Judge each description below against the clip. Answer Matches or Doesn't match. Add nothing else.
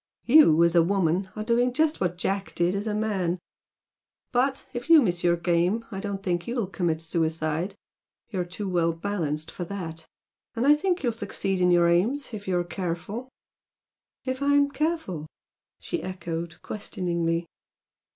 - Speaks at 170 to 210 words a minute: Doesn't match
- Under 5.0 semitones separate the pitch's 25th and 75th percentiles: Doesn't match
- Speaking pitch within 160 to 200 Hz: Matches